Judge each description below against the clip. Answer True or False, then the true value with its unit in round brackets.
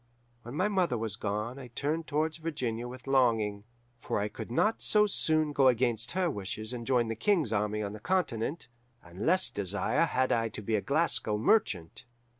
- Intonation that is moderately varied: False (6.5 semitones)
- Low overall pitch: True (120 Hz)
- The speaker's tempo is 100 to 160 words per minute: False (190 wpm)